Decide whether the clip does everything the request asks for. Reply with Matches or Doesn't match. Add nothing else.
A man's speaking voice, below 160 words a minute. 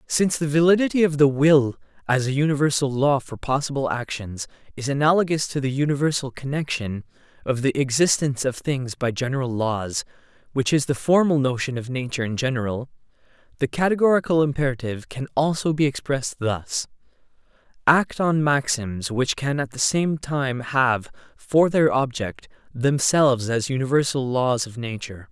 Matches